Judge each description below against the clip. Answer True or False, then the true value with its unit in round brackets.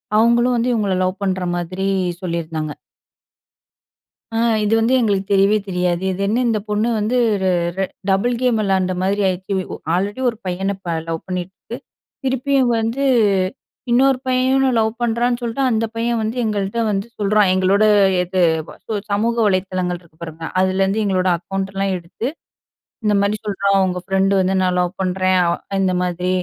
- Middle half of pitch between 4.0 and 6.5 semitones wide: False (3.5 semitones)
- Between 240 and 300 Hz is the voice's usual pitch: False (195 Hz)